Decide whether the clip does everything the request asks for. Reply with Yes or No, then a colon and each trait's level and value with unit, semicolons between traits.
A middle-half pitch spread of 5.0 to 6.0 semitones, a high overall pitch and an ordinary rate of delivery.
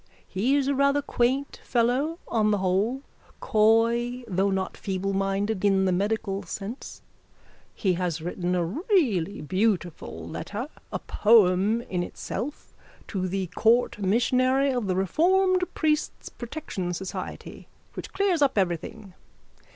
No: wide, 5.4 semitones; high, 210 Hz; slow, 130 wpm